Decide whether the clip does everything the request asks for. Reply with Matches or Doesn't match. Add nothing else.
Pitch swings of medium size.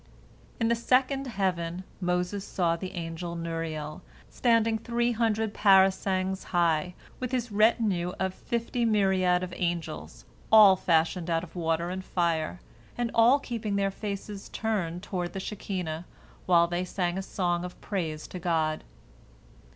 Matches